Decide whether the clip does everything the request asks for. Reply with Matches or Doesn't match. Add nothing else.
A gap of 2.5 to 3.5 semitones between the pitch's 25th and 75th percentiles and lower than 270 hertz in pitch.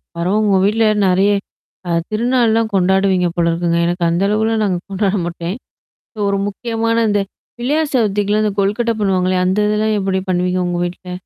Matches